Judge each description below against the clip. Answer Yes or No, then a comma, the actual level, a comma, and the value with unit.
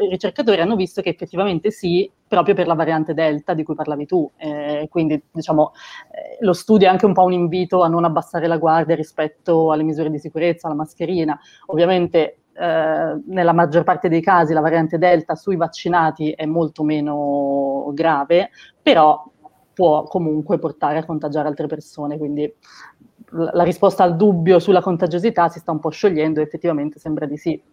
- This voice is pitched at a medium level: Yes, medium, 165 Hz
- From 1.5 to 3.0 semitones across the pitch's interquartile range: Yes, average, 2.7 semitones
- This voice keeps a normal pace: No, fast, 175 wpm